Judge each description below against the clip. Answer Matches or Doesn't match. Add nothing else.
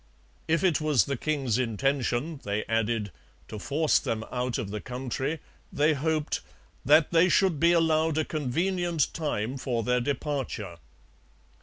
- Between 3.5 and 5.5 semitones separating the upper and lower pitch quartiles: Matches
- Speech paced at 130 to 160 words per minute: Matches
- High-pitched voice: Doesn't match